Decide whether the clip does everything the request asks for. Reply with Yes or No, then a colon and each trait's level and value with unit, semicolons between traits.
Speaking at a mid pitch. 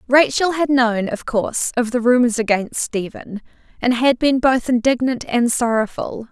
No: high, 245 Hz